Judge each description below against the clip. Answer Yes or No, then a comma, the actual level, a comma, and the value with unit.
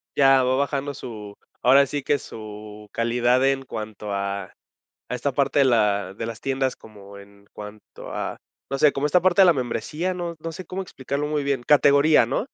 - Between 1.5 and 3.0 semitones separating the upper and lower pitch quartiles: No, average, 5.1 semitones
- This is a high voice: No, low, 130 Hz